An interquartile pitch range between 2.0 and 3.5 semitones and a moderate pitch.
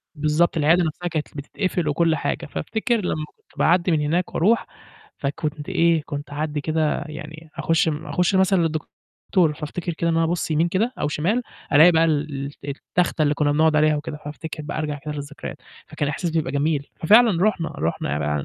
Yes: narrow, 2.6 semitones; medium, 160 Hz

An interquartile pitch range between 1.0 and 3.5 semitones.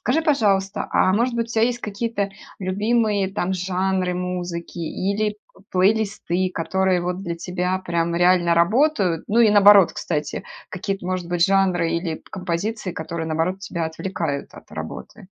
Yes: average, 3.0 semitones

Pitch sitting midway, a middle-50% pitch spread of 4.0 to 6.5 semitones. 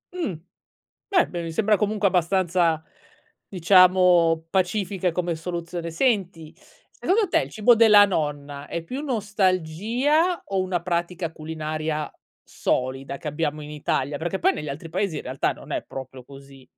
Yes: medium, 175 Hz; average, 4.5 semitones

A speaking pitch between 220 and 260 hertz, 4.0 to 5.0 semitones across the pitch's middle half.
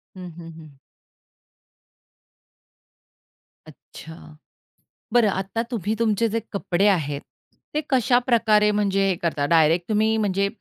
No: high, 200 Hz; average, 4.6 semitones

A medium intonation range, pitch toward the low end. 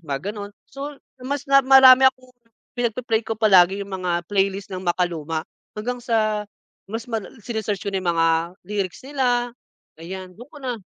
No: average, 4.9 semitones; high, 215 Hz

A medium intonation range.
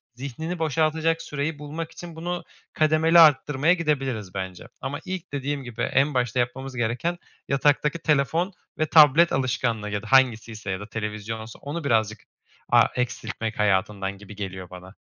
No: wide, 6.2 semitones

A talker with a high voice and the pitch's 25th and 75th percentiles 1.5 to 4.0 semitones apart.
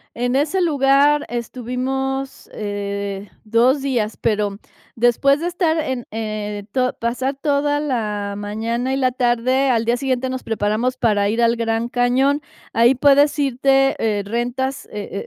Yes: high, 245 Hz; average, 3.4 semitones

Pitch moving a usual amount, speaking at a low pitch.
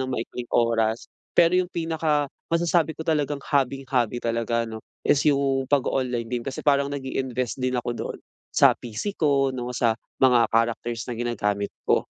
Yes: average, 3.3 semitones; low, 130 Hz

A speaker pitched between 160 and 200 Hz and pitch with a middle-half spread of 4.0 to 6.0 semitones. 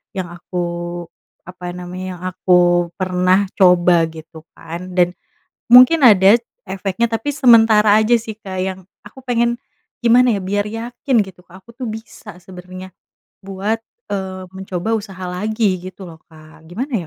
No: high, 190 Hz; average, 3.6 semitones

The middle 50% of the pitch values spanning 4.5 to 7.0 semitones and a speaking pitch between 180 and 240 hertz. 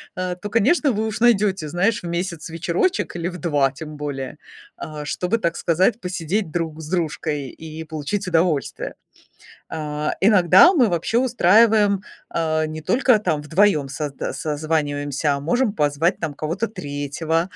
No: average, 5.0 semitones; medium, 170 Hz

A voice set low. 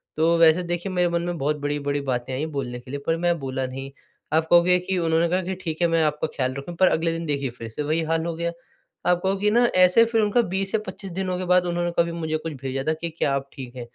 No: medium, 165 Hz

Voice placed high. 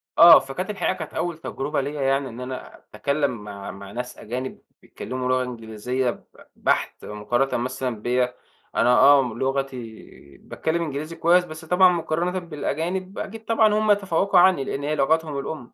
No: medium, 140 Hz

